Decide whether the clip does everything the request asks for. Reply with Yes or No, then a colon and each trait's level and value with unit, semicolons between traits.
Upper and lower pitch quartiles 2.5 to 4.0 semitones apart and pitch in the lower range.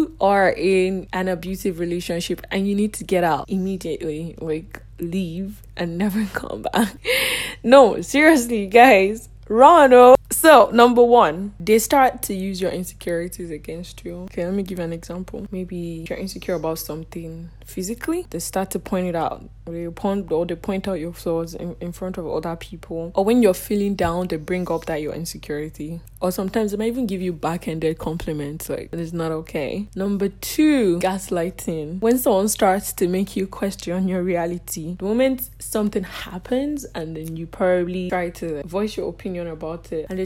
No: average, 3.4 semitones; medium, 185 Hz